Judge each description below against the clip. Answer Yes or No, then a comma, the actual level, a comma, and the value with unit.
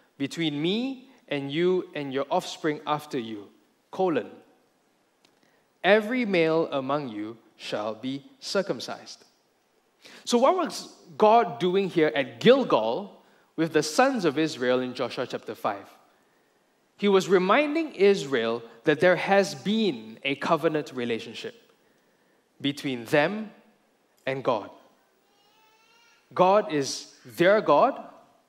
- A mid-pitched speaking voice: Yes, medium, 165 Hz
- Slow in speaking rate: Yes, slow, 110 wpm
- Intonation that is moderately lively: No, wide, 7.1 semitones